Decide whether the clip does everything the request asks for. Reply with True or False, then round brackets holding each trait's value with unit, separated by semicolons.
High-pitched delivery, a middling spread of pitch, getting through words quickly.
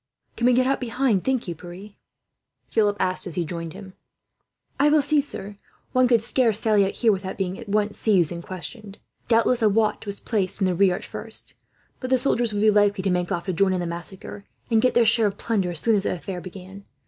True (205 Hz; 3.8 semitones; 235 wpm)